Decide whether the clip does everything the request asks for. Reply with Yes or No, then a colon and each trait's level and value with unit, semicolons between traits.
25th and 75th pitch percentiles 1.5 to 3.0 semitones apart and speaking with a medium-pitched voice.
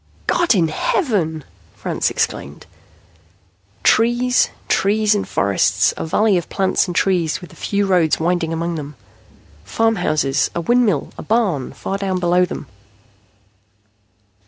No: average, 4.7 semitones; medium, 180 Hz